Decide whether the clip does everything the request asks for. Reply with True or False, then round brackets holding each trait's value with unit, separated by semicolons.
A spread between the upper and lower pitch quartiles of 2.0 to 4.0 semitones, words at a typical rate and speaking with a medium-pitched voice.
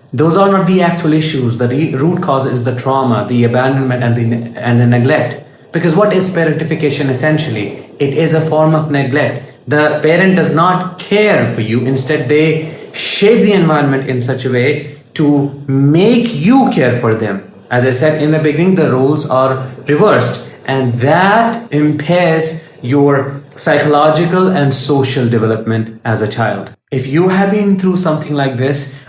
True (3.7 semitones; 170 wpm; 145 Hz)